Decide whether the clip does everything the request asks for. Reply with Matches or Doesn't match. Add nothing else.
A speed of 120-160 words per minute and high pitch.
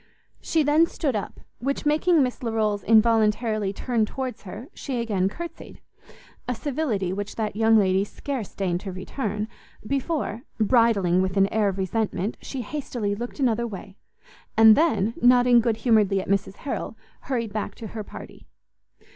Matches